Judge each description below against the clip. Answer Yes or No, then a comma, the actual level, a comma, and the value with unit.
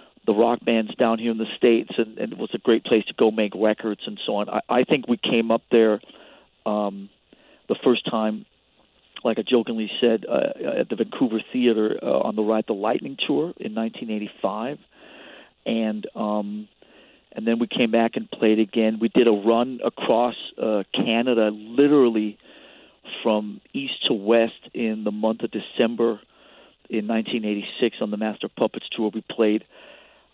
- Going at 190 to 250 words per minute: No, average, 170 wpm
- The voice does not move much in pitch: Yes, narrow, 1.3 semitones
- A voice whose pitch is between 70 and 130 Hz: Yes, low, 110 Hz